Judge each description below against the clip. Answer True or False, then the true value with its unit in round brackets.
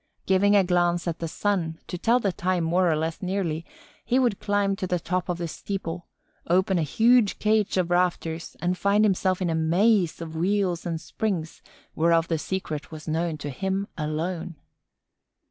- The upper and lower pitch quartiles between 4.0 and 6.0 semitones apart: False (3.1 semitones)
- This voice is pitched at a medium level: True (180 Hz)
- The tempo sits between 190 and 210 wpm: False (180 wpm)